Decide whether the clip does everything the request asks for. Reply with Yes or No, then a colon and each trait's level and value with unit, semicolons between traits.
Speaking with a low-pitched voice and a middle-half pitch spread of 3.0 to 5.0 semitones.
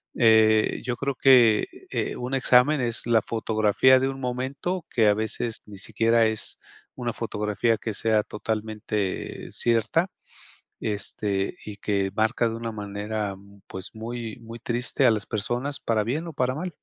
No: low, 115 Hz; narrow, 2.6 semitones